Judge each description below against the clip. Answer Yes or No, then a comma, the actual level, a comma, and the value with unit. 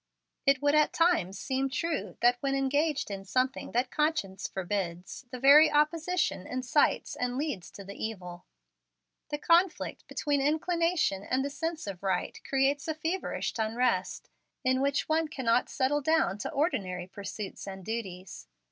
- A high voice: Yes, very high, 265 Hz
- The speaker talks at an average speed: Yes, average, 150 wpm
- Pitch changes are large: Yes, wide, 7.3 semitones